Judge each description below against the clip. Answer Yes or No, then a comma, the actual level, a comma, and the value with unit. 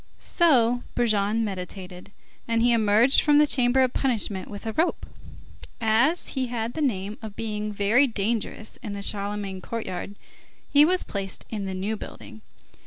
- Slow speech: No, average, 160 wpm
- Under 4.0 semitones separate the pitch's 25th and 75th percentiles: Yes, average, 3.3 semitones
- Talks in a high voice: Yes, high, 220 Hz